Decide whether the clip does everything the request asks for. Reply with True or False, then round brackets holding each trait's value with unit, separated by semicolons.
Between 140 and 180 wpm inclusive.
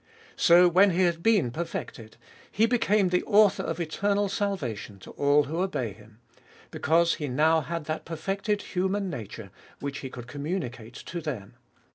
True (160 wpm)